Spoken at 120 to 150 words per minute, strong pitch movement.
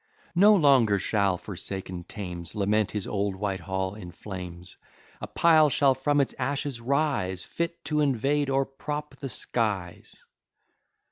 Yes: slow, 135 wpm; wide, 7.0 semitones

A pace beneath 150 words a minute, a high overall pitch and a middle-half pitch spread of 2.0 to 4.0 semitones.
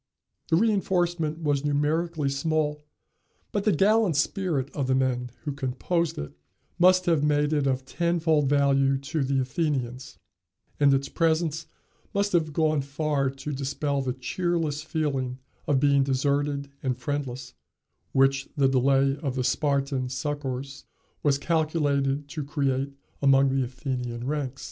No: average, 140 wpm; medium, 140 Hz; narrow, 2.6 semitones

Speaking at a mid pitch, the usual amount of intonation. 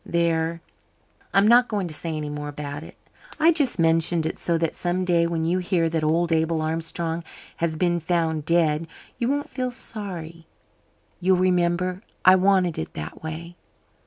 No: medium, 170 Hz; narrow, 2.2 semitones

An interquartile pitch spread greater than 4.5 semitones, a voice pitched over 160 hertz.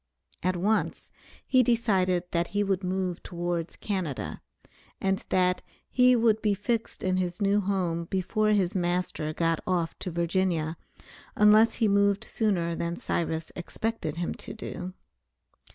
No: average, 3.2 semitones; medium, 185 Hz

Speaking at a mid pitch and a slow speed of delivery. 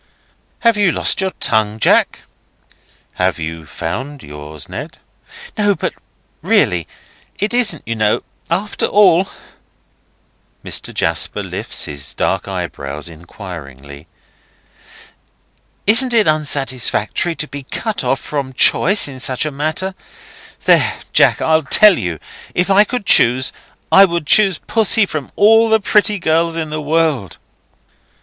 Yes: medium, 155 Hz; slow, 130 wpm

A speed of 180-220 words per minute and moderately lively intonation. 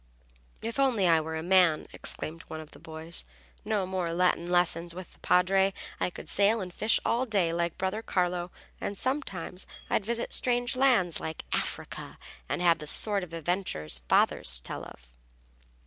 No: average, 170 wpm; average, 3.6 semitones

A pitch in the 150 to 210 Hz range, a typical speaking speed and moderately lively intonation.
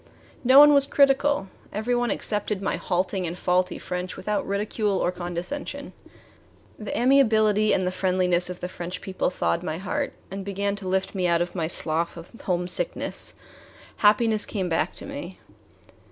Yes: high, 190 Hz; average, 165 wpm; average, 3.4 semitones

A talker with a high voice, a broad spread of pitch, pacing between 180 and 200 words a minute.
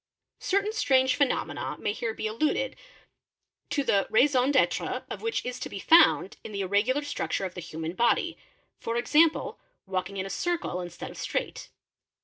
No: high, 245 Hz; wide, 7.0 semitones; average, 165 wpm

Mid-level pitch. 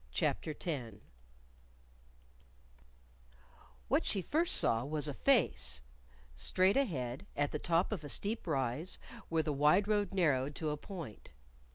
Yes: medium, 155 Hz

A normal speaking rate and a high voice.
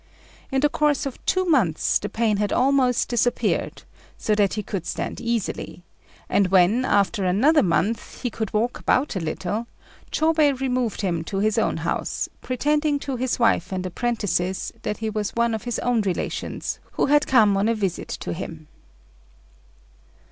Yes: average, 170 wpm; high, 225 Hz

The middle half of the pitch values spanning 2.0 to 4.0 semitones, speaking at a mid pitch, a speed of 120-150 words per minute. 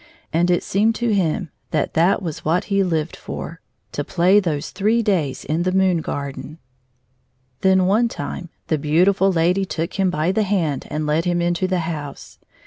No: average, 3.4 semitones; medium, 175 Hz; average, 185 wpm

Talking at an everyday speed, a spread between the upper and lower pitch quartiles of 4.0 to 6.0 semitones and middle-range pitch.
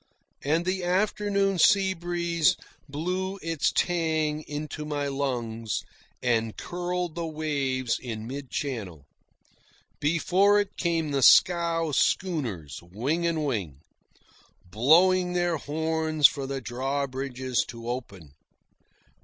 No: slow, 105 wpm; average, 5.1 semitones; medium, 150 Hz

